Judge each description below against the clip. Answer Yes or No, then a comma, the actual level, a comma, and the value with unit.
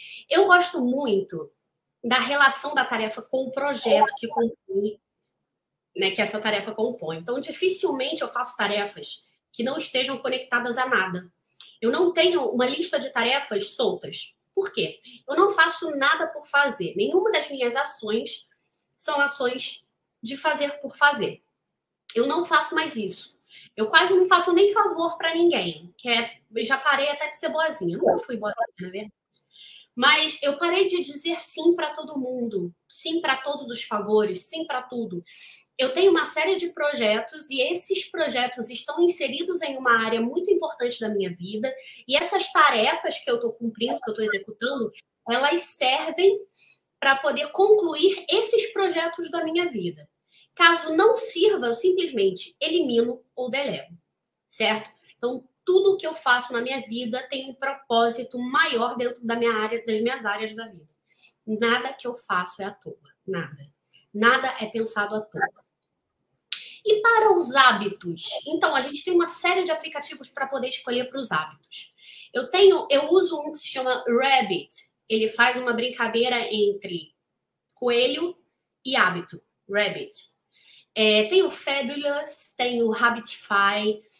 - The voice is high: Yes, very high, 265 Hz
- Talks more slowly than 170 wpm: Yes, average, 160 wpm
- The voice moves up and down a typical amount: No, wide, 6.0 semitones